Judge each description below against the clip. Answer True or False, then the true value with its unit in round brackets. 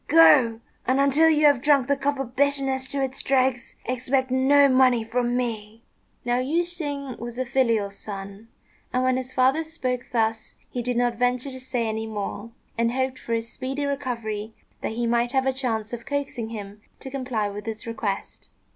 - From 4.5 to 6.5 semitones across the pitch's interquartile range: False (2.8 semitones)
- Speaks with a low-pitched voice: False (250 Hz)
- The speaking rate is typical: True (190 wpm)